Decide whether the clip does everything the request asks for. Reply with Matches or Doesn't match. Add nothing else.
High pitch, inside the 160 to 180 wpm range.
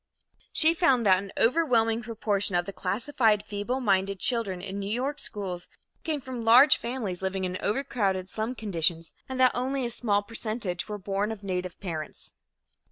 Matches